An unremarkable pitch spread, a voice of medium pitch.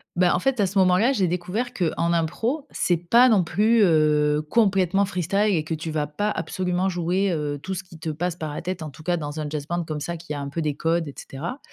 Yes: average, 3.7 semitones; medium, 175 Hz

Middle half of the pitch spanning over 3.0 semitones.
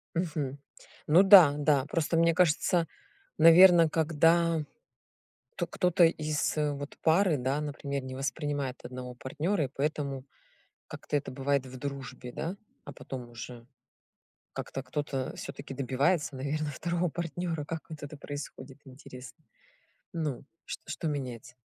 Yes: average, 3.6 semitones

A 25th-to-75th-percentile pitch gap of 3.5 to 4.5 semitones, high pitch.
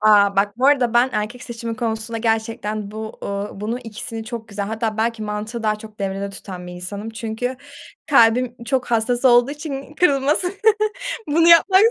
No: average, 2.8 semitones; high, 225 Hz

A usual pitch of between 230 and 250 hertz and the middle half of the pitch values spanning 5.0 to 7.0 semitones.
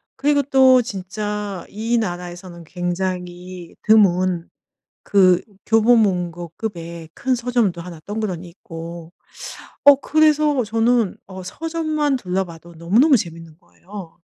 No: high, 190 Hz; average, 5.3 semitones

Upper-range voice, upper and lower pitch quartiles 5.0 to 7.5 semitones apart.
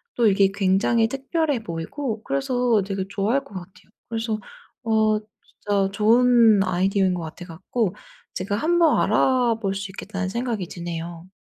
No: high, 210 Hz; average, 3.8 semitones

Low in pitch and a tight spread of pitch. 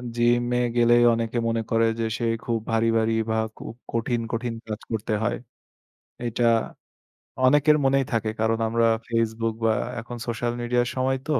Yes: low, 115 Hz; narrow, 1.2 semitones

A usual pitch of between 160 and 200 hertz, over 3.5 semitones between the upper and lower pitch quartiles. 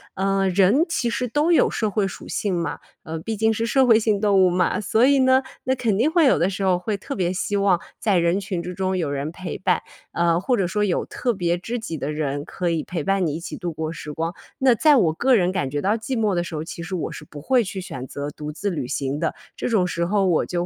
Yes: medium, 185 Hz; average, 4.7 semitones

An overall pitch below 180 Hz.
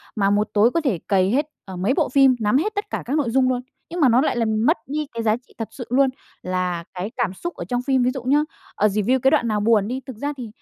No: high, 245 Hz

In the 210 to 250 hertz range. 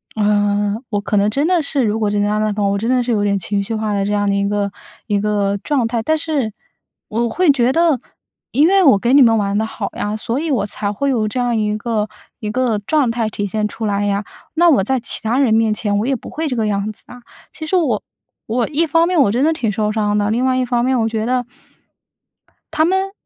Yes: high, 225 Hz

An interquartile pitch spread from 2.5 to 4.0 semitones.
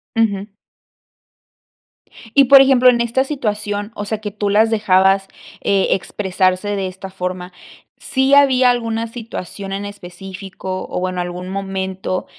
Yes: average, 3.3 semitones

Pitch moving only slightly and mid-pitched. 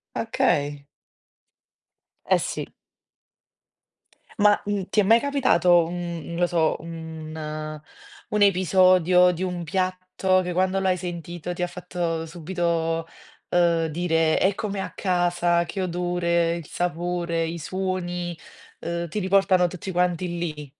Yes: narrow, 1.8 semitones; medium, 175 Hz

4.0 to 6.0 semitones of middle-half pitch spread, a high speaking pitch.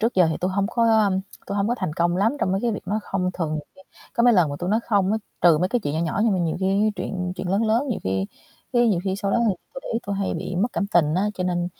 No: average, 3.4 semitones; high, 195 Hz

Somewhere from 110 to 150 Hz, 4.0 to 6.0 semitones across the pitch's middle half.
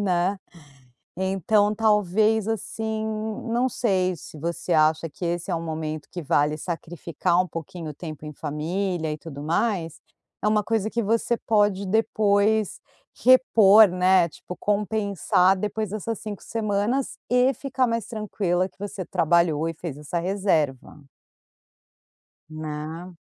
No: high, 190 Hz; average, 4.5 semitones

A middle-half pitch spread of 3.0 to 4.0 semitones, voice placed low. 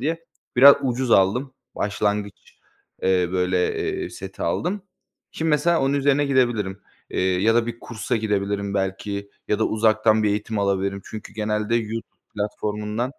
Yes: average, 3.4 semitones; low, 105 Hz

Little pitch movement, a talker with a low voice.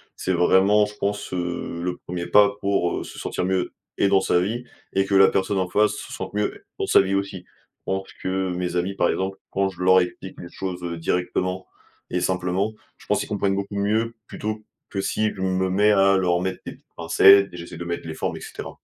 Yes: narrow, 1.7 semitones; very low, 95 Hz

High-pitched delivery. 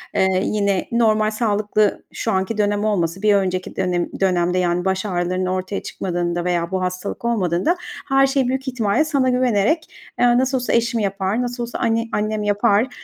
Yes: high, 205 Hz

